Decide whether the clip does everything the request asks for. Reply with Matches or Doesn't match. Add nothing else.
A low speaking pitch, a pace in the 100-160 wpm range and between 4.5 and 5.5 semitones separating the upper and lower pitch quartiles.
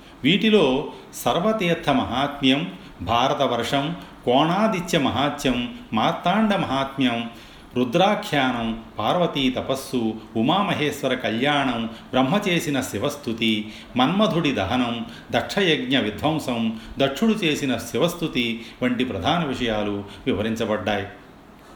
Doesn't match